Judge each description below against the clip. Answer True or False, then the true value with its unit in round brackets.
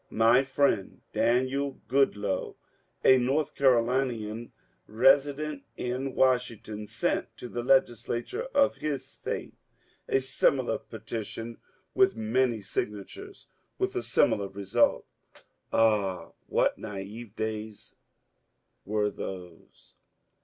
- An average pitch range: True (3.9 semitones)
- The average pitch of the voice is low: True (120 Hz)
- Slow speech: True (95 wpm)